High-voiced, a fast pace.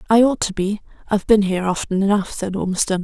Yes: high, 200 Hz; fast, 220 wpm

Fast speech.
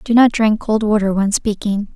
Yes: fast, 215 wpm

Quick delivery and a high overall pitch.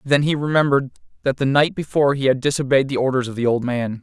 No: fast, 240 wpm; low, 135 Hz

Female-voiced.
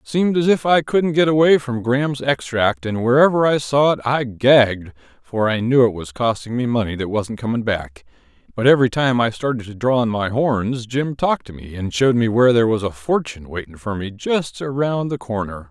No: male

